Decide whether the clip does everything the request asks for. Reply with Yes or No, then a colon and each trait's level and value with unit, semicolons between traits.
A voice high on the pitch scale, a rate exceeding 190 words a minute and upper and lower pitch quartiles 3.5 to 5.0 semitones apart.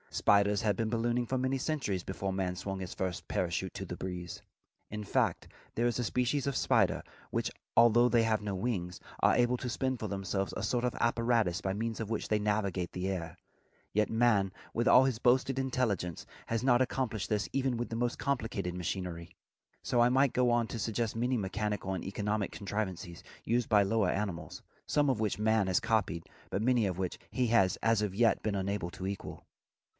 No: low, 110 Hz; average, 200 wpm; average, 3.9 semitones